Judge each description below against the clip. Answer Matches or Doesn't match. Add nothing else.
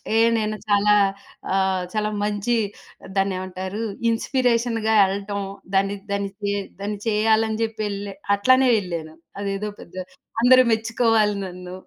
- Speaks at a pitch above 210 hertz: Doesn't match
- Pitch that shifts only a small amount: Matches